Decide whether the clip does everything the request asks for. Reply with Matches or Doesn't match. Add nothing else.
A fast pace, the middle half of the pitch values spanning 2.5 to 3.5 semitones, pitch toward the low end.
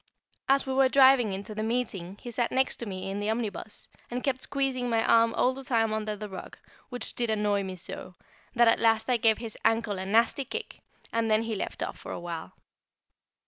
Doesn't match